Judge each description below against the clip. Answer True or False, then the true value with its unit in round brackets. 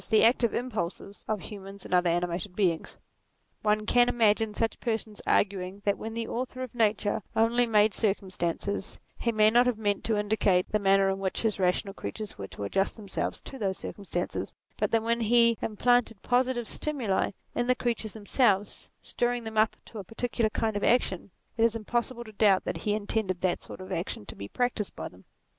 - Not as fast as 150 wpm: False (190 wpm)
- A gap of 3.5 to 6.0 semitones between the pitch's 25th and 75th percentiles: False (3.0 semitones)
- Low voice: False (215 Hz)